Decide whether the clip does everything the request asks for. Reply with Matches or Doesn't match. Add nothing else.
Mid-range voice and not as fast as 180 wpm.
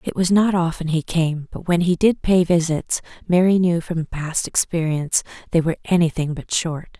Doesn't match